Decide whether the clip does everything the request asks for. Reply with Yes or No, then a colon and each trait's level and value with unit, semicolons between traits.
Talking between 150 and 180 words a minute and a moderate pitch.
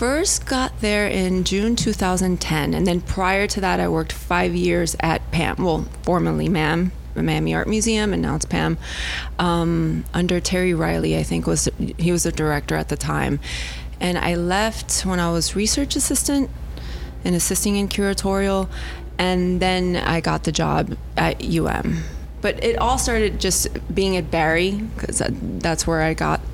Yes: average, 170 wpm; medium, 175 Hz